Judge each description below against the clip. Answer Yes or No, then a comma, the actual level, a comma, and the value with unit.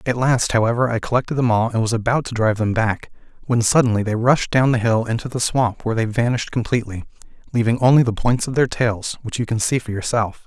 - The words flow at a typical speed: No, fast, 235 wpm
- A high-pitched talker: No, low, 115 Hz